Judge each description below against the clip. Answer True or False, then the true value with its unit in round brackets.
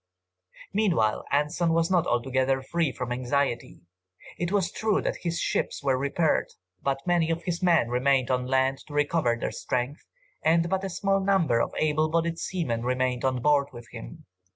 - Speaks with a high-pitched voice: False (145 Hz)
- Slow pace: False (175 wpm)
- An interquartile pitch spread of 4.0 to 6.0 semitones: True (4.9 semitones)